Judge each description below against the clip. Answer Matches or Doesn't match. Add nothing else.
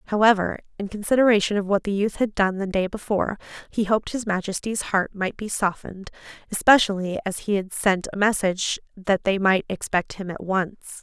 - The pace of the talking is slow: Doesn't match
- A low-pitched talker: Doesn't match